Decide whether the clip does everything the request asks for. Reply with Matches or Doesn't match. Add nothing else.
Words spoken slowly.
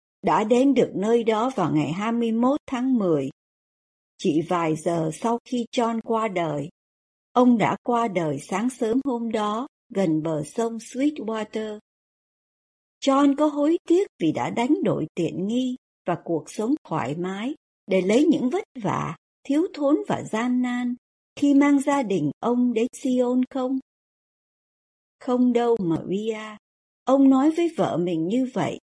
Matches